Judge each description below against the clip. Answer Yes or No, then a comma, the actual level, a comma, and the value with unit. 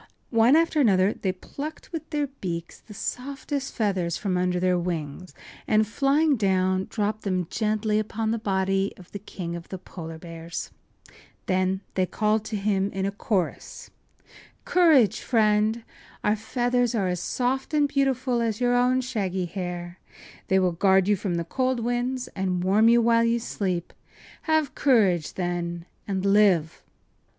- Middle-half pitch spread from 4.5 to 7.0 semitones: Yes, average, 4.8 semitones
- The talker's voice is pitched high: Yes, high, 210 Hz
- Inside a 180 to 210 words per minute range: No, average, 160 wpm